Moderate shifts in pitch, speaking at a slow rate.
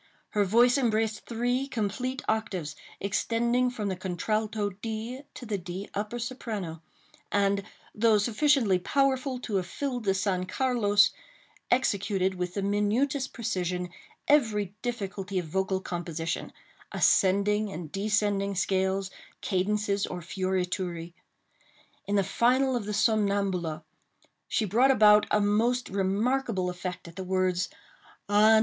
Yes: average, 3.6 semitones; slow, 125 wpm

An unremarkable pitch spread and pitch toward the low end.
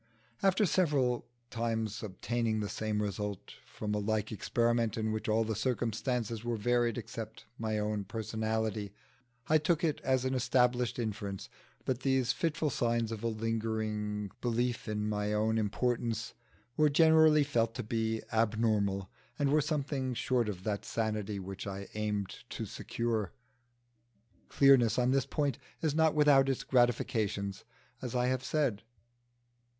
Yes: average, 3.3 semitones; low, 115 Hz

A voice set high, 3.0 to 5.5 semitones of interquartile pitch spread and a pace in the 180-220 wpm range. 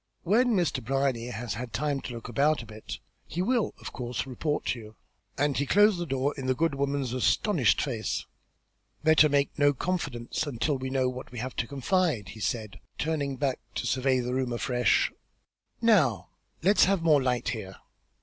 No: low, 135 Hz; average, 4.0 semitones; average, 190 wpm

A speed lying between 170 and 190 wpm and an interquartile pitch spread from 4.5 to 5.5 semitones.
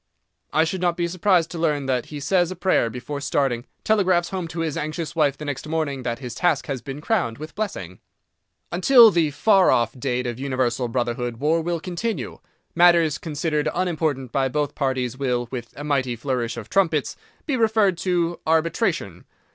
Yes: average, 175 wpm; average, 5.1 semitones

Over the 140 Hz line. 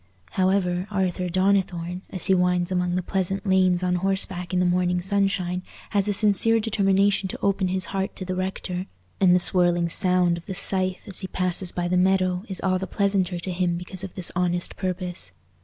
Yes: medium, 185 Hz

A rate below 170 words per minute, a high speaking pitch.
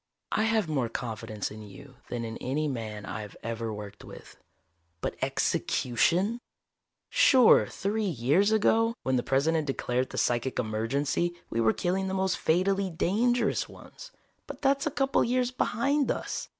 No: average, 150 wpm; medium, 160 Hz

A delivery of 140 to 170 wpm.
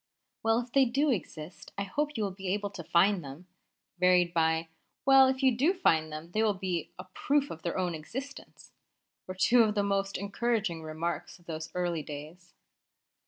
No: average, 190 wpm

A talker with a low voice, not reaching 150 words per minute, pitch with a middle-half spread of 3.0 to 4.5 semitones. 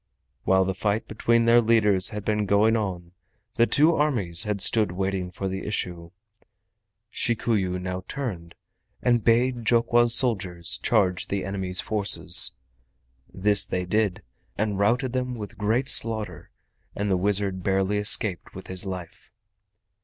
Yes: low, 100 Hz; average, 140 wpm; average, 3.5 semitones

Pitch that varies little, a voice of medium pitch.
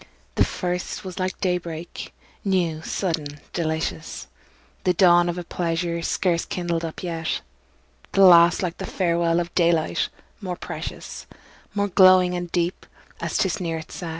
Yes: narrow, 1.5 semitones; medium, 175 Hz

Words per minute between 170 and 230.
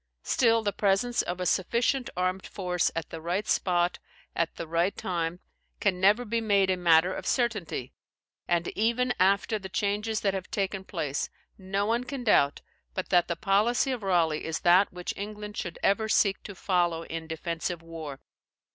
Yes: average, 175 wpm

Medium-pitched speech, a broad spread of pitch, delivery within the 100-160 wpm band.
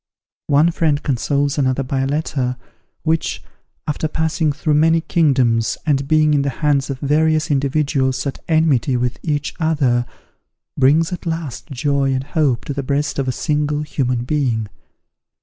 No: medium, 145 Hz; average, 2.7 semitones; average, 155 wpm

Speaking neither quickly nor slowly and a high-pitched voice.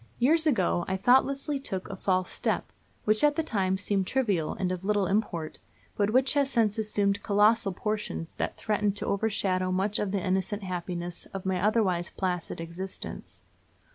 Yes: average, 170 wpm; high, 200 Hz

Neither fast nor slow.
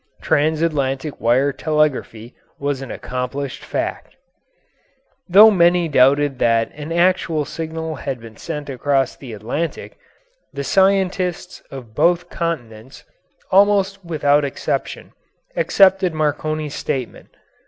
No: slow, 105 wpm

